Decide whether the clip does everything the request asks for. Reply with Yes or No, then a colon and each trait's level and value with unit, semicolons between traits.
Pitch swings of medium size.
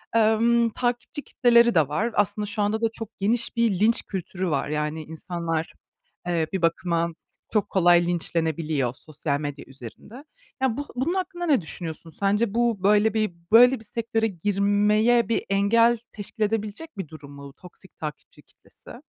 No: wide, 5.7 semitones